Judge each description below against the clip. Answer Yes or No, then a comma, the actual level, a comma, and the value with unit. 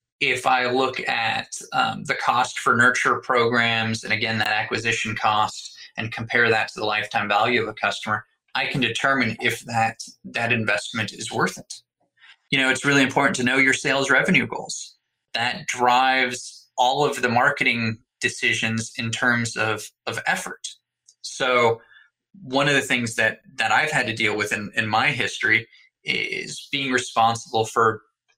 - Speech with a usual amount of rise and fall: No, narrow, 2.3 semitones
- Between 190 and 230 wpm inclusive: No, average, 165 wpm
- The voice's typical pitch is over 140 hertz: No, low, 120 Hz